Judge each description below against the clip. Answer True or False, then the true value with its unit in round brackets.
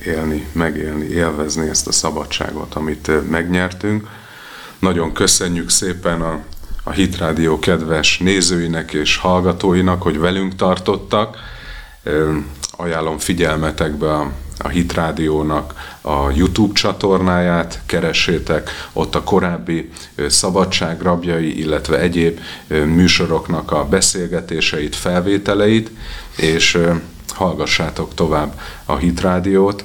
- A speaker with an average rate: False (95 wpm)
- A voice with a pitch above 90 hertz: False (85 Hz)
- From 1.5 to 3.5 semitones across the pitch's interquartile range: True (3.0 semitones)